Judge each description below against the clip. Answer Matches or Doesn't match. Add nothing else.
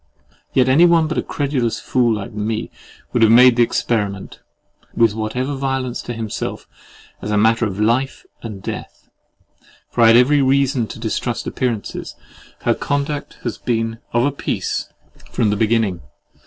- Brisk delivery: Doesn't match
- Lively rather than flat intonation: Doesn't match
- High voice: Doesn't match